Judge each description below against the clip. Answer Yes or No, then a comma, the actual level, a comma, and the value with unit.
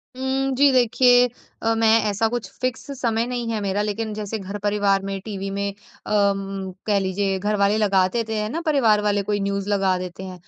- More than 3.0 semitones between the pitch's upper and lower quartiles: No, narrow, 2.4 semitones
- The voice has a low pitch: No, high, 205 Hz